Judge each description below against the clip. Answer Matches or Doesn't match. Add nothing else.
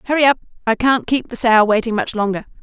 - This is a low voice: Doesn't match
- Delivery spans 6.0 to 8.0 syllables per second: Matches